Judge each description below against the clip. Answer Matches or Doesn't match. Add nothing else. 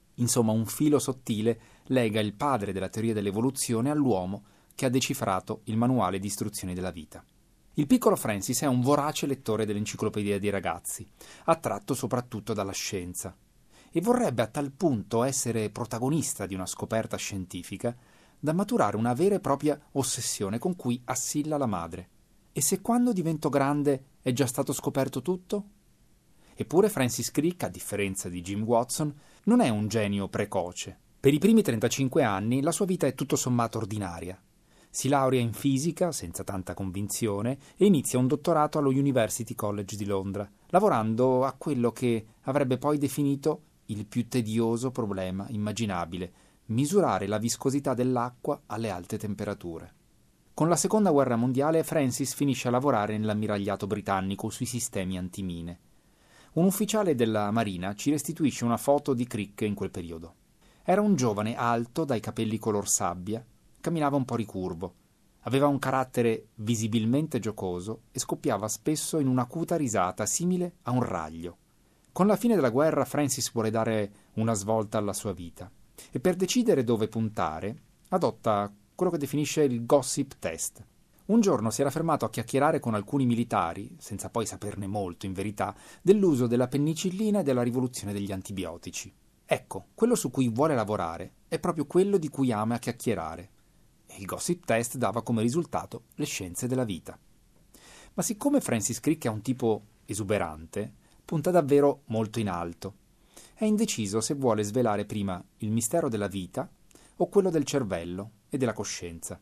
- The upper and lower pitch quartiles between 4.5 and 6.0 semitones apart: Matches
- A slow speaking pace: Doesn't match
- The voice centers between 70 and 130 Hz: Matches